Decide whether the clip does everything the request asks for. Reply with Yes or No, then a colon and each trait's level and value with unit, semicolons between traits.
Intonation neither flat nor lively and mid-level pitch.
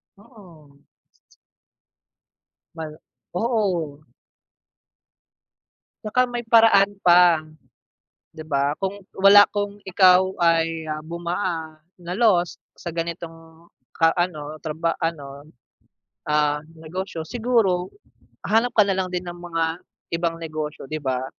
Yes: average, 3.6 semitones; medium, 170 Hz